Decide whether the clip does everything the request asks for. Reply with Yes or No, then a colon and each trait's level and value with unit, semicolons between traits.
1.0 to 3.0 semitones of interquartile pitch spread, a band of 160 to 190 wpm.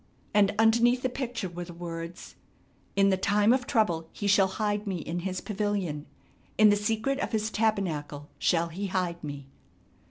No: average, 4.0 semitones; average, 170 wpm